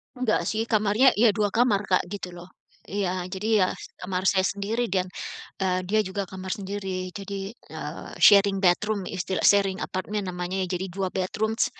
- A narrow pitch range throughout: Yes, narrow, 2.0 semitones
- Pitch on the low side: No, high, 195 Hz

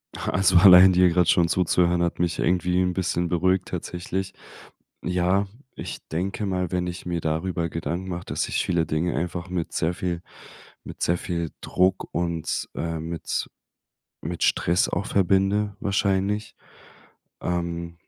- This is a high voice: No, very low, 90 Hz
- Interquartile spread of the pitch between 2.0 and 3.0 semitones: No, narrow, 1.5 semitones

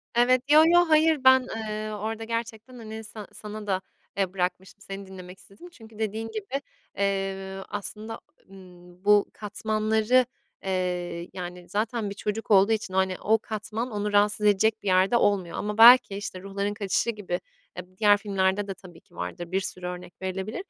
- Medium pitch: No, high, 205 Hz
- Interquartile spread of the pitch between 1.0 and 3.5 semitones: Yes, average, 2.7 semitones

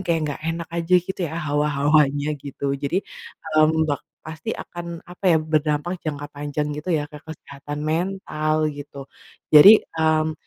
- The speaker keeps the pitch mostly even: Yes, narrow, 1.8 semitones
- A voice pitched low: No, medium, 155 Hz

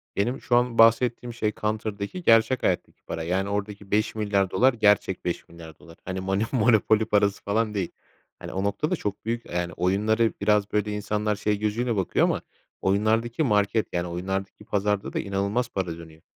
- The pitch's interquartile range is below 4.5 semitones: Yes, narrow, 2.5 semitones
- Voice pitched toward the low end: Yes, low, 105 Hz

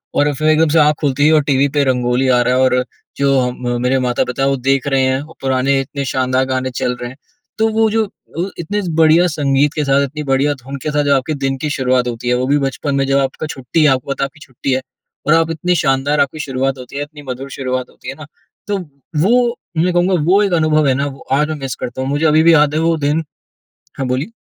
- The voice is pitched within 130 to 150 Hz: Yes, medium, 140 Hz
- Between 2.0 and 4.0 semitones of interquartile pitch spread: Yes, average, 2.8 semitones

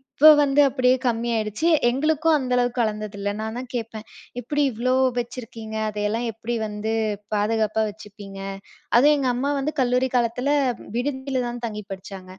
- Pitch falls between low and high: No, high, 235 Hz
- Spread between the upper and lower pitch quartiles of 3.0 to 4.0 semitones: Yes, average, 3.3 semitones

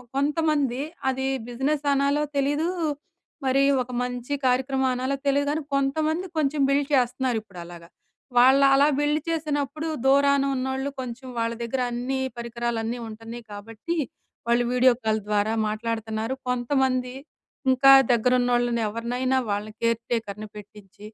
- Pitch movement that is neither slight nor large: Yes, average, 3.1 semitones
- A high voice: Yes, very high, 255 Hz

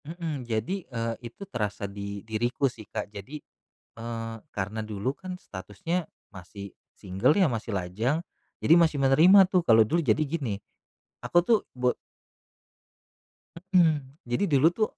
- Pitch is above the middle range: No, low, 125 Hz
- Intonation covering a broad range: Yes, wide, 7.4 semitones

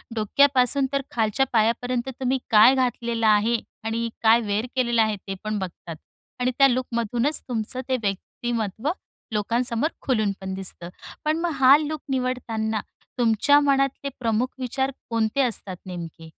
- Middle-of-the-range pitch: No, high, 235 Hz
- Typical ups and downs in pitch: Yes, average, 3.3 semitones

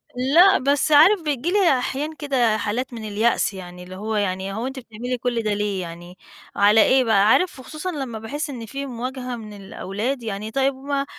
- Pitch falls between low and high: No, high, 240 Hz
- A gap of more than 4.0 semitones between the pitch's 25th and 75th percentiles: Yes, average, 4.8 semitones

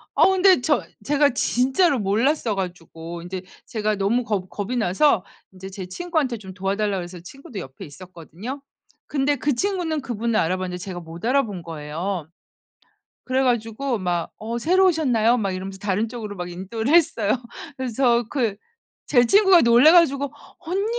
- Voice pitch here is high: Yes, high, 225 Hz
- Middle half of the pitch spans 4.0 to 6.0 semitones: No, wide, 6.6 semitones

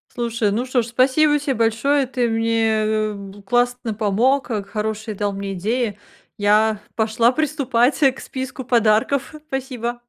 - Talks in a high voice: Yes, high, 230 Hz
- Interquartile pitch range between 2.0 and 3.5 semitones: Yes, average, 3.1 semitones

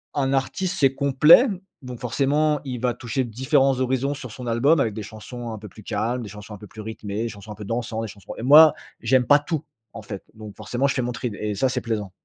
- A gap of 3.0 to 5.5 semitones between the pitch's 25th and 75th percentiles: Yes, average, 3.7 semitones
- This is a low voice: Yes, low, 120 Hz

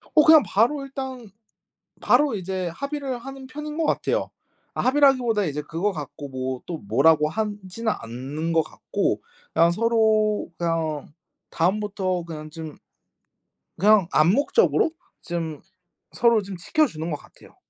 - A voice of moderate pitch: No, high, 195 Hz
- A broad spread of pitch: Yes, wide, 7.3 semitones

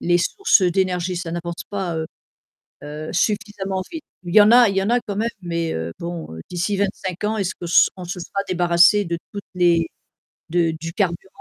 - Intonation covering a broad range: No, average, 2.8 semitones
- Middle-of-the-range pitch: Yes, medium, 180 Hz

